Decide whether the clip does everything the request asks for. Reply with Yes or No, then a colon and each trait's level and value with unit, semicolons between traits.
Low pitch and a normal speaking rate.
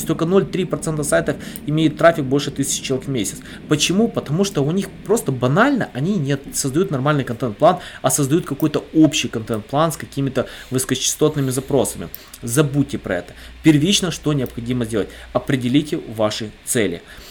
No: medium, 145 Hz; average, 140 wpm